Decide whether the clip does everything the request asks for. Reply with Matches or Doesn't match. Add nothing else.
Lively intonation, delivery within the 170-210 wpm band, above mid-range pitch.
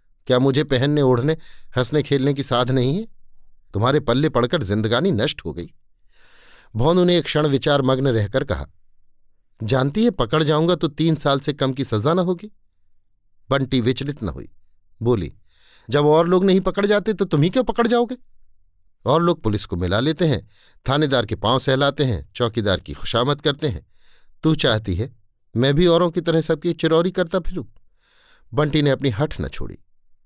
Doesn't match